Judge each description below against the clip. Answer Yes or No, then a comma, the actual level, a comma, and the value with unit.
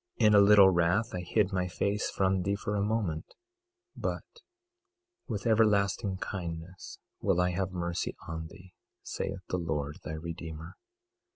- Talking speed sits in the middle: Yes, average, 155 wpm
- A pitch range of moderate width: Yes, average, 3.0 semitones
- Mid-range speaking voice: No, very low, 95 Hz